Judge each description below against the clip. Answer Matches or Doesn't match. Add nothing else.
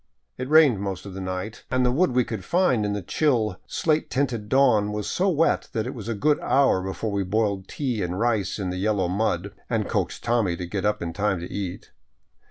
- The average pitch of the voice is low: Matches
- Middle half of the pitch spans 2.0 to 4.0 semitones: Doesn't match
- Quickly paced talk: Matches